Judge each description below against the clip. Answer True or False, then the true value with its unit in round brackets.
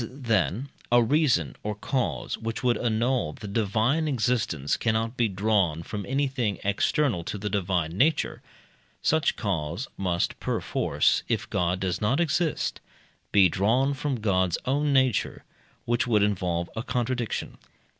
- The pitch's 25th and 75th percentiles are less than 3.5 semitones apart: False (5.1 semitones)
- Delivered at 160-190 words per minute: False (140 wpm)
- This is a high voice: False (110 Hz)